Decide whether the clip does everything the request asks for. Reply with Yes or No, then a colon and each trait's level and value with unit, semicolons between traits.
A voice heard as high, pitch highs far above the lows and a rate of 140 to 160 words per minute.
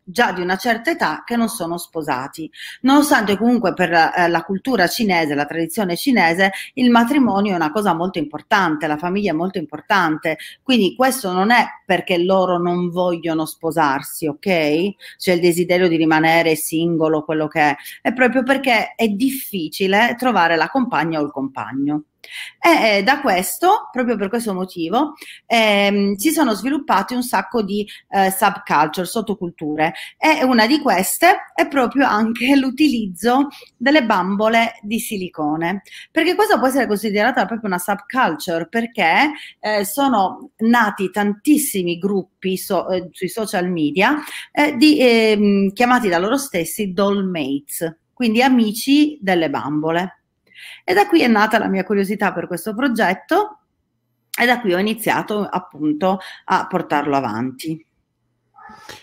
Yes: high, 200 Hz; wide, 6.3 semitones; average, 145 wpm